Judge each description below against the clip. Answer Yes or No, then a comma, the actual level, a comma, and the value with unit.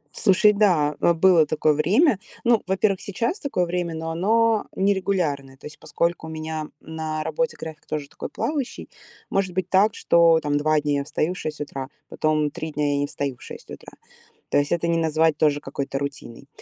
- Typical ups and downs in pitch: Yes, average, 4.1 semitones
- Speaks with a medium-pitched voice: Yes, medium, 160 Hz